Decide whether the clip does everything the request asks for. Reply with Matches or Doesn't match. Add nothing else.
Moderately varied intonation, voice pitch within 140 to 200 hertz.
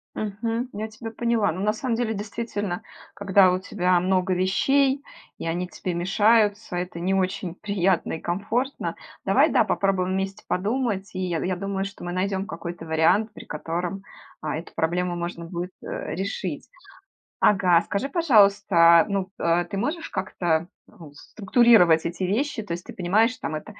Matches